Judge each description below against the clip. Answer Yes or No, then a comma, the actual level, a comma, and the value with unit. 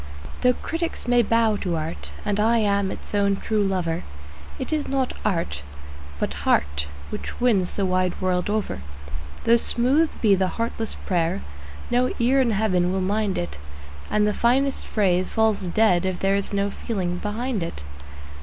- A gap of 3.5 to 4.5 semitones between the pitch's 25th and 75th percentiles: Yes, average, 4.0 semitones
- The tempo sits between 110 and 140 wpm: No, average, 165 wpm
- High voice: Yes, high, 205 Hz